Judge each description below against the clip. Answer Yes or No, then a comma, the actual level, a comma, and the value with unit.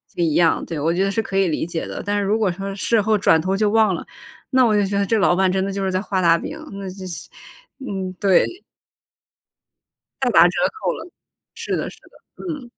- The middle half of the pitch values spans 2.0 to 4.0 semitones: Yes, narrow, 2.5 semitones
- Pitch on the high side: Yes, high, 195 Hz